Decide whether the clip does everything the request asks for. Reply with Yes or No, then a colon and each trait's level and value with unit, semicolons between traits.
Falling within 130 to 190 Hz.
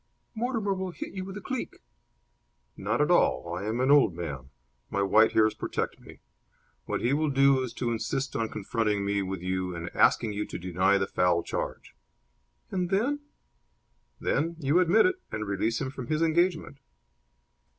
No: low, 120 Hz